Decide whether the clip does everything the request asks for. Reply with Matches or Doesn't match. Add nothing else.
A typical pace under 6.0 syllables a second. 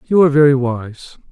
Matches